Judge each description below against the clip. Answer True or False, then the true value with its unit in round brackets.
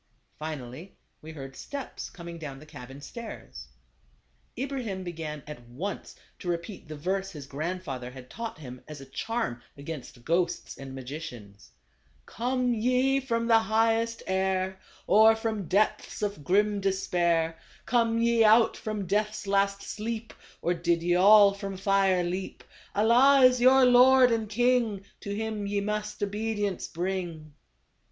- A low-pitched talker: False (195 Hz)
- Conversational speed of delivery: True (145 wpm)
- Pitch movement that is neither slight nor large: False (5.7 semitones)